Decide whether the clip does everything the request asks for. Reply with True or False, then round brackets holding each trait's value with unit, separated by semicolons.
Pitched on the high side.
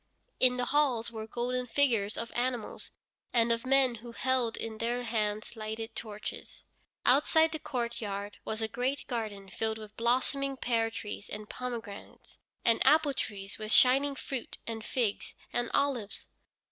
True (235 Hz)